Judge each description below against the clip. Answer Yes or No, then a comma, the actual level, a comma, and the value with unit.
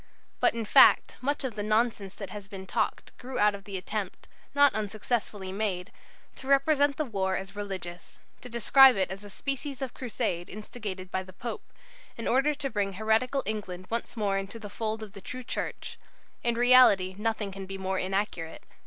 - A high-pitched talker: Yes, high, 210 Hz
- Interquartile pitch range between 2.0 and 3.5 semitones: No, average, 4.1 semitones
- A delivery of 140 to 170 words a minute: No, average, 190 wpm